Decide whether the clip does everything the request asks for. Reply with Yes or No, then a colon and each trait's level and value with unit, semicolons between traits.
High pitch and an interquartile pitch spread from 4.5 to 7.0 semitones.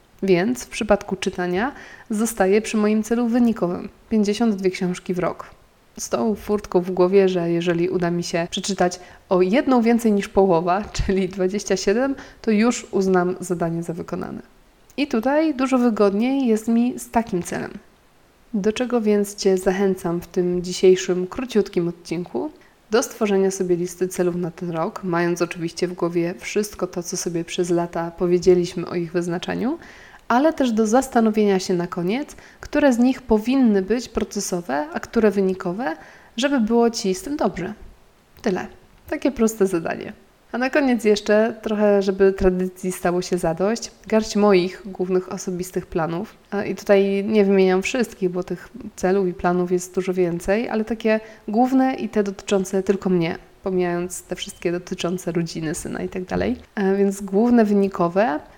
No: high, 195 Hz; average, 3.5 semitones